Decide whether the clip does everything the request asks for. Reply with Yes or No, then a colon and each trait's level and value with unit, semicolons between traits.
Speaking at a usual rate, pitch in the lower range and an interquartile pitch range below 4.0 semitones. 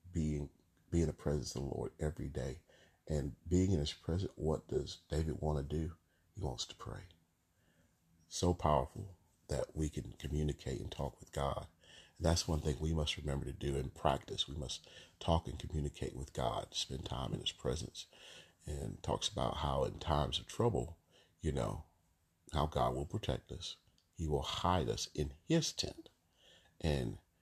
Yes: average, 180 wpm; very low, 80 Hz; average, 2.8 semitones